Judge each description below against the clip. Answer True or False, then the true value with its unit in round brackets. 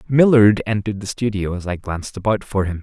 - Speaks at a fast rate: True (210 wpm)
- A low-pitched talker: True (105 Hz)